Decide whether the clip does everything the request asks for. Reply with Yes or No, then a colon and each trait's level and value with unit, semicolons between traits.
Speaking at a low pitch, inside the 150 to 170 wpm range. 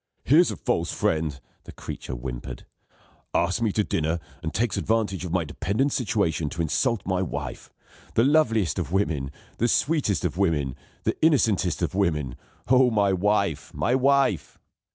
Yes: very low, 95 Hz; average, 155 wpm